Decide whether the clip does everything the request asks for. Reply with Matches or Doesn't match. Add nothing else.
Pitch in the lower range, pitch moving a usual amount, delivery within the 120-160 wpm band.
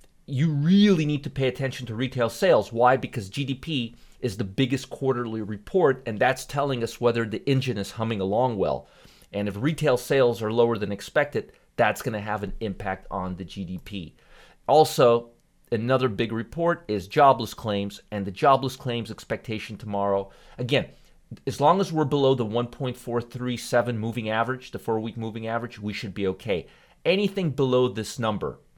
Doesn't match